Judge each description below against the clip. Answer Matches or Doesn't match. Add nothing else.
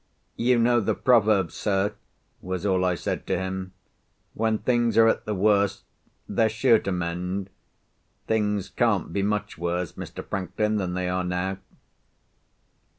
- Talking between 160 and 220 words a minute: Doesn't match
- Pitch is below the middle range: Matches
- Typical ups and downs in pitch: Matches